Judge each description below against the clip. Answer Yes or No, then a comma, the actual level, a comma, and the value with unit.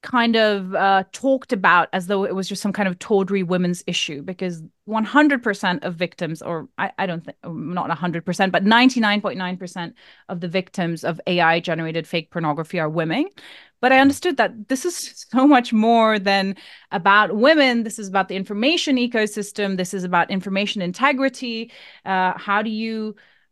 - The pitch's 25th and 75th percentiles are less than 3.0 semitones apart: No, average, 4.1 semitones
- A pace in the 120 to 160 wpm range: No, average, 170 wpm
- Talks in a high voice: Yes, high, 200 Hz